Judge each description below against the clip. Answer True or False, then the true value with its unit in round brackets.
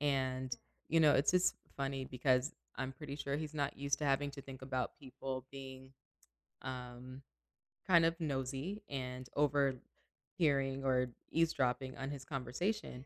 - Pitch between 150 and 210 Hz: False (135 Hz)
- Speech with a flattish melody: True (1.9 semitones)